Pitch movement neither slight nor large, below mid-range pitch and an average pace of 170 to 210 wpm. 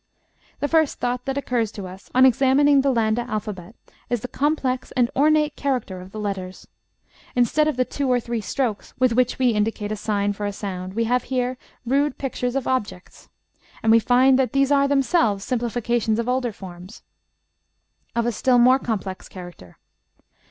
No: average, 4.0 semitones; high, 245 Hz; average, 180 wpm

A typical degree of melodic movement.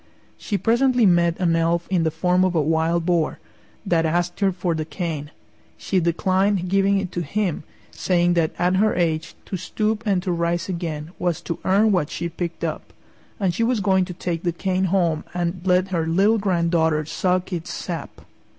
No: narrow, 2.3 semitones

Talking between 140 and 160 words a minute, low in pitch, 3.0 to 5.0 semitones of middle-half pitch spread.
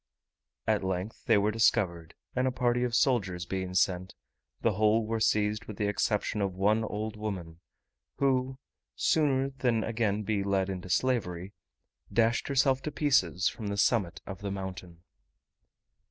Yes: average, 155 wpm; low, 105 Hz; average, 4.0 semitones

